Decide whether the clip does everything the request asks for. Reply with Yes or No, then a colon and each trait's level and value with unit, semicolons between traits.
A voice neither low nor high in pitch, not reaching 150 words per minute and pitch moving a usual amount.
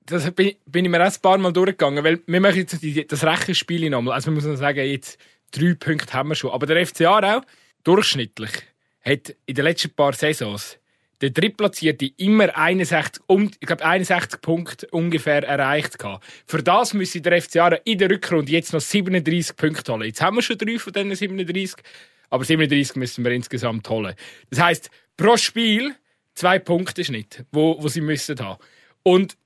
No: medium, 165 Hz; average, 175 wpm; average, 4.5 semitones